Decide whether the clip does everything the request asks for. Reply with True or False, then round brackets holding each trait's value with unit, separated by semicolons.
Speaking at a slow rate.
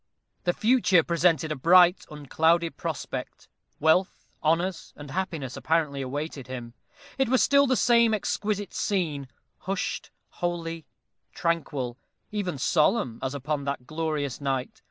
True (125 wpm)